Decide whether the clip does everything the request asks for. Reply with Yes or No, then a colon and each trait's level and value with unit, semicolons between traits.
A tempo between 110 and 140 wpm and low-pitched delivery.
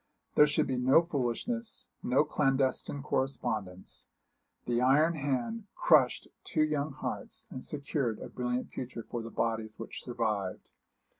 Yes: slow, 135 wpm; low, 130 Hz